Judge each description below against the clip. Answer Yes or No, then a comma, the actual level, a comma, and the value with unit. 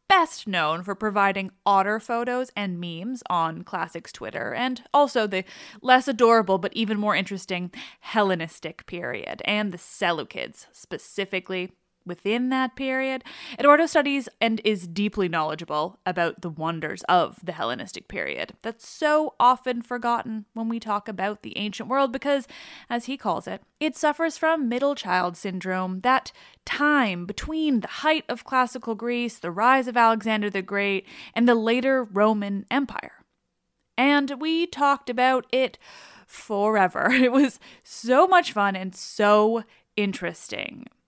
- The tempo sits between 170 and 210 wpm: No, average, 140 wpm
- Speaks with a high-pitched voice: Yes, high, 230 Hz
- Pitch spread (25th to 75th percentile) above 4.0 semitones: Yes, average, 5.0 semitones